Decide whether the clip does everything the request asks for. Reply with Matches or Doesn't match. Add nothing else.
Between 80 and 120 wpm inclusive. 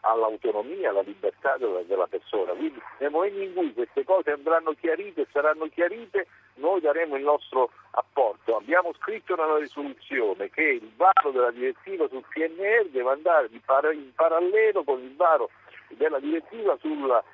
Doesn't match